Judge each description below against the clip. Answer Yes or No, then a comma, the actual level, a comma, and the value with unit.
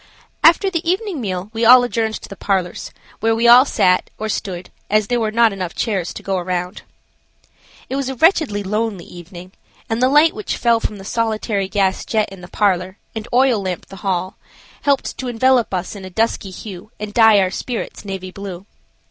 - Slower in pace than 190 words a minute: No, average, 195 wpm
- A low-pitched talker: No, high, 215 Hz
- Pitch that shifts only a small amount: No, average, 4.0 semitones